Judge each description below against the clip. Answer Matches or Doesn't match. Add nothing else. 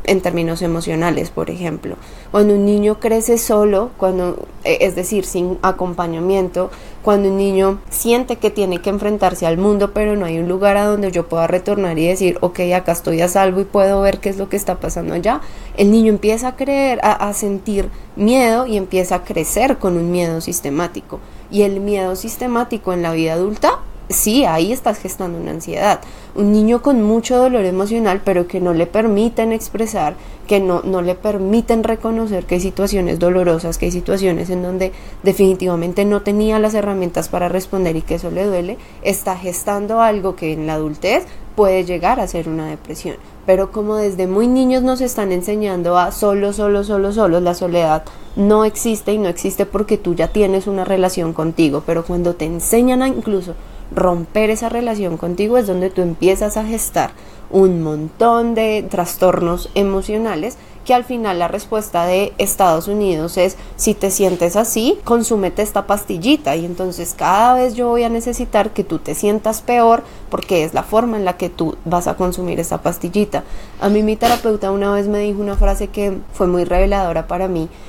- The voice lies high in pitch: Matches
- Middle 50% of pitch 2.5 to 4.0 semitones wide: Matches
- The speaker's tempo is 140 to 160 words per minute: Doesn't match